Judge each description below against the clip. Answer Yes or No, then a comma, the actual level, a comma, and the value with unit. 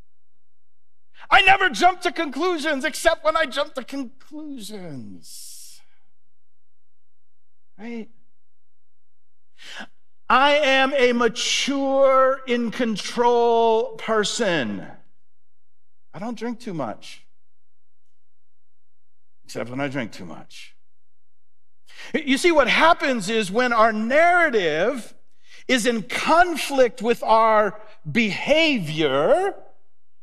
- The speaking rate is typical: No, slow, 85 wpm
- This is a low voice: No, high, 220 Hz